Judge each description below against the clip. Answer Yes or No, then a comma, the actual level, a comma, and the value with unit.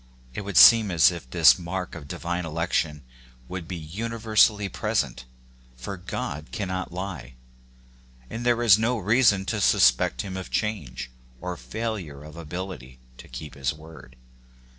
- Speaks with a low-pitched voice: Yes, very low, 90 Hz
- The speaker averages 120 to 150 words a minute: Yes, average, 145 wpm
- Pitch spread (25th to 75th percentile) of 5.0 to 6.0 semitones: Yes, average, 5.3 semitones